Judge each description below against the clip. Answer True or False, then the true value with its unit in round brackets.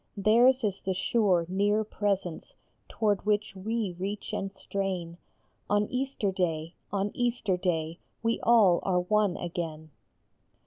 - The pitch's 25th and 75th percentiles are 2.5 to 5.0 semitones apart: True (3.0 semitones)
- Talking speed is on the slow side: True (130 wpm)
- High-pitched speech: True (195 Hz)